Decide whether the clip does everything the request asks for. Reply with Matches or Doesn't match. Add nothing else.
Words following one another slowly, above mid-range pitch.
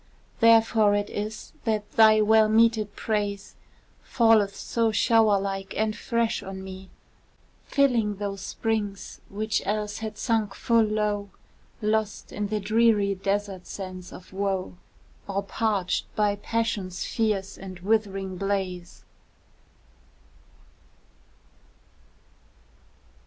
Matches